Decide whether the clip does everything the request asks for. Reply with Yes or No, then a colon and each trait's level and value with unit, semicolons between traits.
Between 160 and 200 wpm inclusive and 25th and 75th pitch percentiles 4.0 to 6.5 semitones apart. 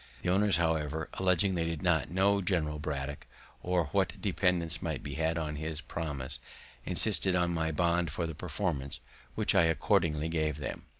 No: average, 170 wpm; average, 2.9 semitones